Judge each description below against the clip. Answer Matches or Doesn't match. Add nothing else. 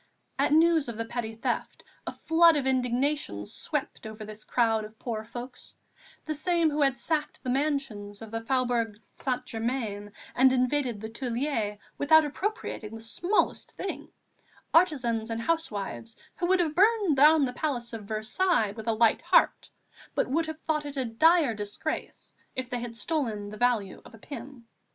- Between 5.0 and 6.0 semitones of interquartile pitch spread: Matches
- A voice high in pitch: Matches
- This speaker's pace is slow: Doesn't match